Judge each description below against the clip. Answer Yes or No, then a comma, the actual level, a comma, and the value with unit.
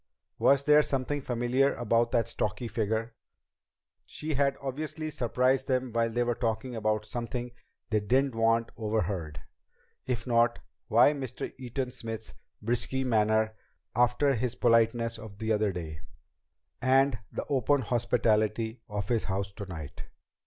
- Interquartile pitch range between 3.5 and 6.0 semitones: No, average, 2.9 semitones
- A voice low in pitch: Yes, low, 115 Hz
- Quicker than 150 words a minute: No, slow, 135 wpm